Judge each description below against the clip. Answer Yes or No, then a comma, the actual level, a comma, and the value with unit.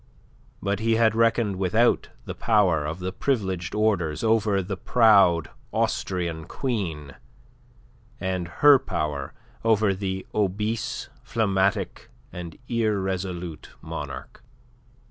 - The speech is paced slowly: Yes, slow, 100 wpm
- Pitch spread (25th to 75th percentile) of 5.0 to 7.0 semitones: No, average, 3.9 semitones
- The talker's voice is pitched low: Yes, very low, 95 Hz